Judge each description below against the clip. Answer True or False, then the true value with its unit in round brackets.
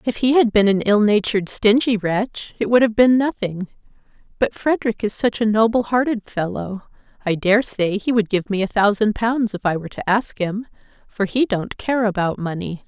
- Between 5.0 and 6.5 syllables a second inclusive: True (5.1 syllables/s)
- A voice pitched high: True (215 Hz)